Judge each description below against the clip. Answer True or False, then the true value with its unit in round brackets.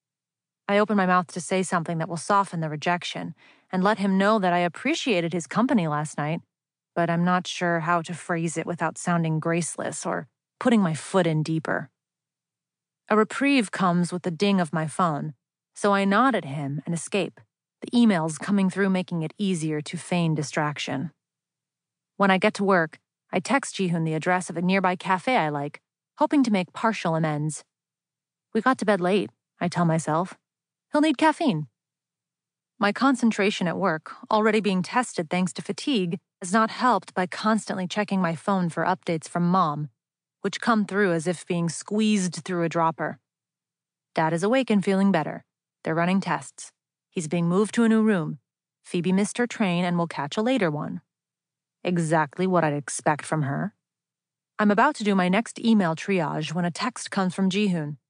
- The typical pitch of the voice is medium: True (180 Hz)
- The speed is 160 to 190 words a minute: True (180 wpm)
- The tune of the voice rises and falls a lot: False (3.9 semitones)